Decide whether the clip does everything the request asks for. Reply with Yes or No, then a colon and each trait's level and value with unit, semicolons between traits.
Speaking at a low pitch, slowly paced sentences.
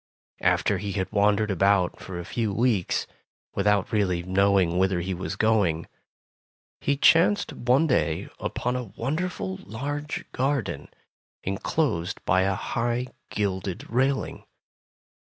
Yes: low, 100 Hz; slow, 120 wpm